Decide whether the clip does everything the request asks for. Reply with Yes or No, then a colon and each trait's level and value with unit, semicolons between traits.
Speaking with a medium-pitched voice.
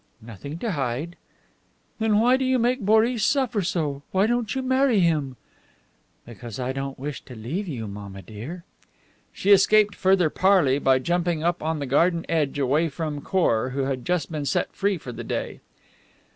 Yes: medium, 160 Hz